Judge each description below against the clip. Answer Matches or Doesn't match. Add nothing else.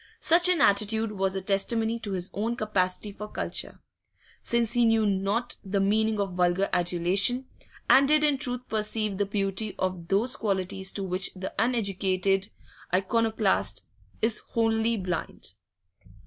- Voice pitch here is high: Matches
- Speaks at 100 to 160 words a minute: Matches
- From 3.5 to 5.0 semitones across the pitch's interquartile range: Doesn't match